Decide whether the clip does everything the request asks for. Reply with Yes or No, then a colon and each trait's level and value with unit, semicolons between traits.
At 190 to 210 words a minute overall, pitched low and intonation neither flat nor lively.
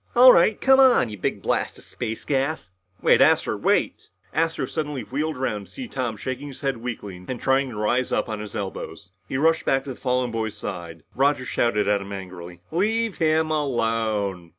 No: average, 195 wpm; low, 125 Hz; wide, 6.1 semitones